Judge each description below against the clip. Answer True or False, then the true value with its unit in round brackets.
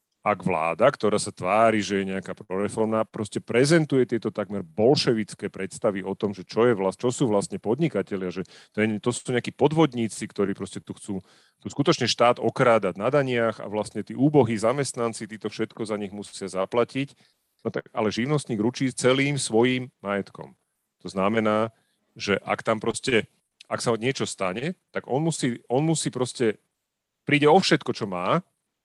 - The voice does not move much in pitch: False (3.8 semitones)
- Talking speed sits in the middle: False (170 wpm)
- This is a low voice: True (115 Hz)